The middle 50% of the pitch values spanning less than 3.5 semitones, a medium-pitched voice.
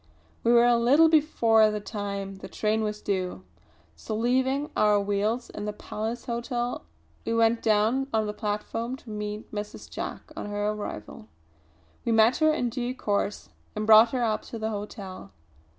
No: narrow, 2.4 semitones; high, 220 Hz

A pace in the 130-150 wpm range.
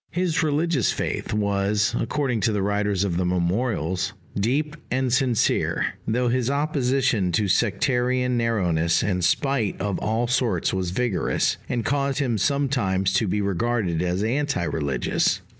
Yes: average, 140 wpm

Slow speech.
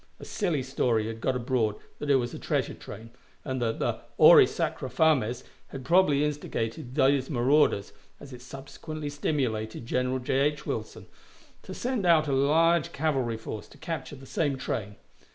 No: average, 165 wpm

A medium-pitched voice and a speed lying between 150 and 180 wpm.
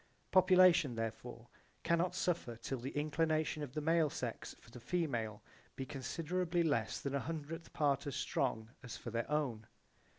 Yes: medium, 145 Hz; average, 160 wpm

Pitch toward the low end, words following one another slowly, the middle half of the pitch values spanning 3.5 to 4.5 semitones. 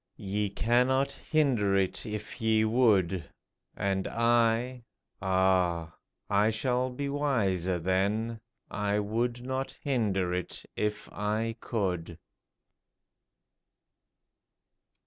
Yes: low, 105 Hz; slow, 100 wpm; average, 4.0 semitones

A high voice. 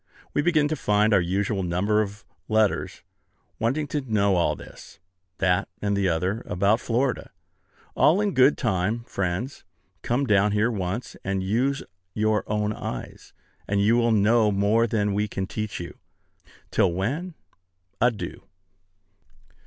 No: low, 105 Hz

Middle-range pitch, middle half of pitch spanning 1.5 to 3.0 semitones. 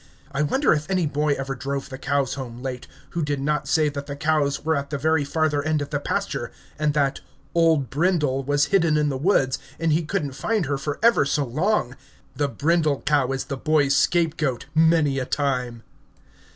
Yes: medium, 145 Hz; narrow, 2.4 semitones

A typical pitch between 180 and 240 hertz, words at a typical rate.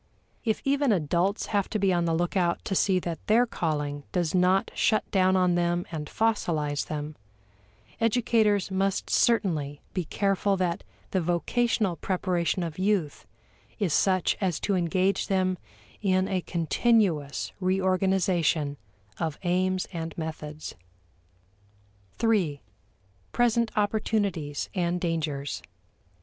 No: medium, 185 Hz; slow, 120 wpm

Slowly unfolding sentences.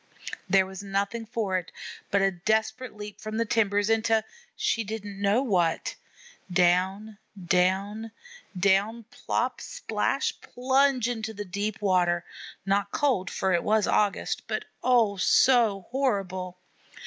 Yes: slow, 130 wpm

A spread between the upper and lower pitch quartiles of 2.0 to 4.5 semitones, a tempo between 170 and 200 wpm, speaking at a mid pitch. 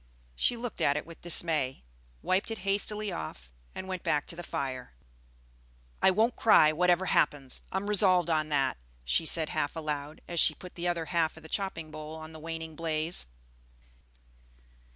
Yes: average, 3.3 semitones; average, 175 wpm; medium, 165 Hz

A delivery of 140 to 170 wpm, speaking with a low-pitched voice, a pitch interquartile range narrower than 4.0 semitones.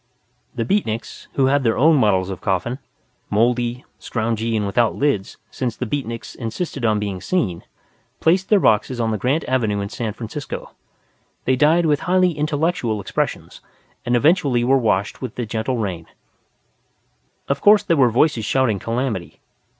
No: average, 160 wpm; low, 120 Hz; average, 4.8 semitones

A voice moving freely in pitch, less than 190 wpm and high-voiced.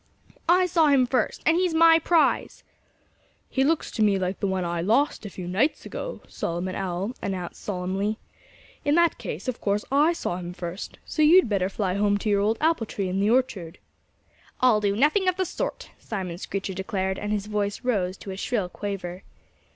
No: wide, 6.6 semitones; average, 195 wpm; high, 205 Hz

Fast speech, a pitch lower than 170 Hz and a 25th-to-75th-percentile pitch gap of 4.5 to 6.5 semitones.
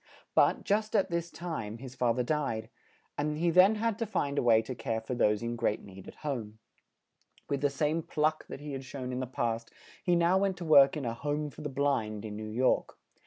Yes: fast, 230 wpm; medium, 140 Hz; wide, 5.5 semitones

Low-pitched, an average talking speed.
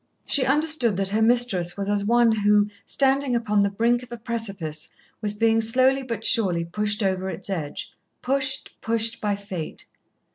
No: high, 220 Hz; average, 170 wpm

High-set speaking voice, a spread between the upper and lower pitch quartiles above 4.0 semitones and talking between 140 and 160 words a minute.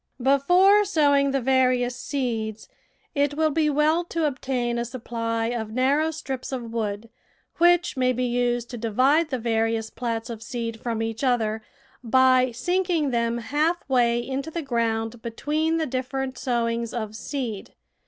No: very high, 250 Hz; average, 3.7 semitones; average, 155 wpm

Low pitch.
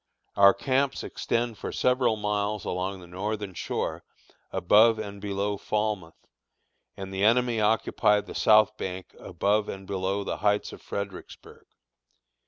Yes: low, 105 Hz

